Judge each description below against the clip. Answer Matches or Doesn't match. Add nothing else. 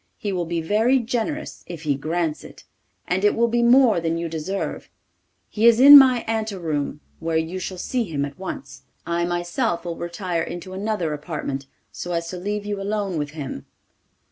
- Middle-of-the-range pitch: Matches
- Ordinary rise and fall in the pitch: Matches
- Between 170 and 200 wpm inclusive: Matches